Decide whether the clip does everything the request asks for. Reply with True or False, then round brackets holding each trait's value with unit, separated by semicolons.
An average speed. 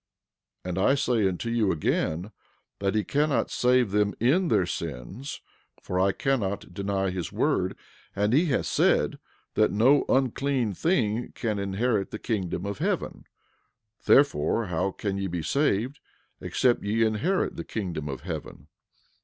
True (150 wpm)